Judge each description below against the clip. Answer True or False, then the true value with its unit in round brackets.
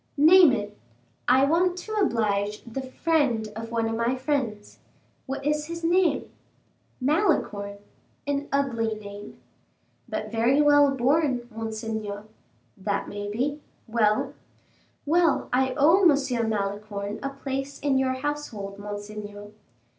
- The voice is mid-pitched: False (250 Hz)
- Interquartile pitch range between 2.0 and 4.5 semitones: False (5.3 semitones)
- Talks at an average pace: False (120 wpm)